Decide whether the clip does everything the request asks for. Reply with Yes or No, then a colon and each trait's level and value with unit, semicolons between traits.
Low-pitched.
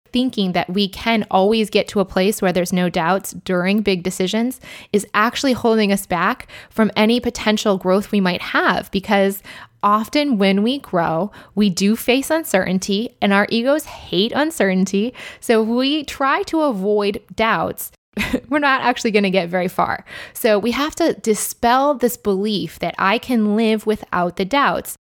No: high, 210 Hz